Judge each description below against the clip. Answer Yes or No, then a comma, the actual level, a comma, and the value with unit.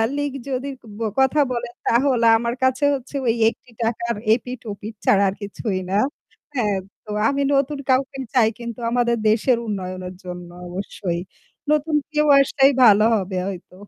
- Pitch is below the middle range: No, high, 235 Hz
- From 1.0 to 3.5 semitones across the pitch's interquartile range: No, average, 4.7 semitones